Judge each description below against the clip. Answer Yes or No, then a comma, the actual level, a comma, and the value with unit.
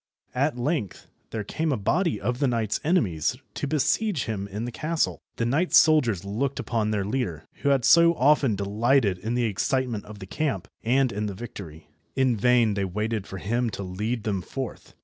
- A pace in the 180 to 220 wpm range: Yes, average, 190 wpm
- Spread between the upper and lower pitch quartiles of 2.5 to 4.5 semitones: No, average, 5.0 semitones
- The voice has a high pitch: No, low, 115 Hz